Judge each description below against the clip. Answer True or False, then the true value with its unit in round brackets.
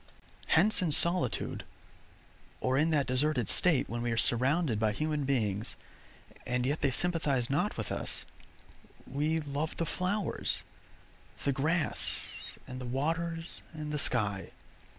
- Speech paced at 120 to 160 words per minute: True (135 wpm)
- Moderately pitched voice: True (145 Hz)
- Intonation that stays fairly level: False (4.4 semitones)